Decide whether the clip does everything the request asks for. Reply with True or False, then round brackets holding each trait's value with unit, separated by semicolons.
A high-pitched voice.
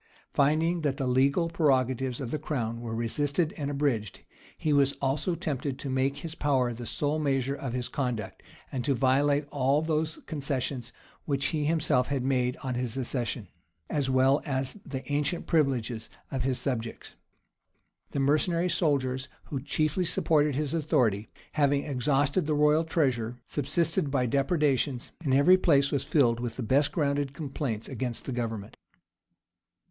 False (140 Hz)